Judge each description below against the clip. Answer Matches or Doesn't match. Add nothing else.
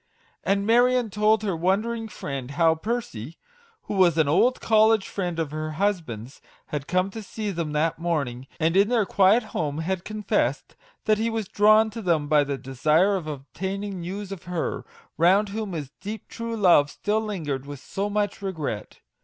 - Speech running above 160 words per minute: Matches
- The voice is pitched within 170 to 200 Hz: Matches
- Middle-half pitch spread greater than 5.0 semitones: Matches